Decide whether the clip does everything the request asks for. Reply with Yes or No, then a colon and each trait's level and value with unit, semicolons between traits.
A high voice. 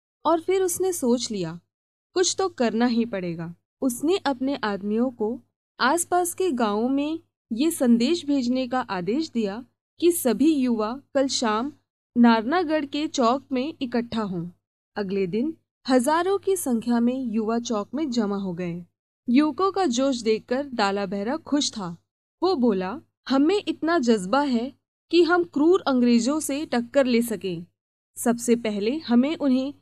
Yes: very high, 255 Hz